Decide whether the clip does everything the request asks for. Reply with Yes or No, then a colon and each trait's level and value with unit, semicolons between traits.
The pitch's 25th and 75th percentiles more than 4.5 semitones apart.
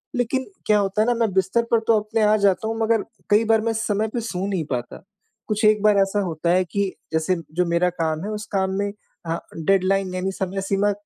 No: average, 2.7 semitones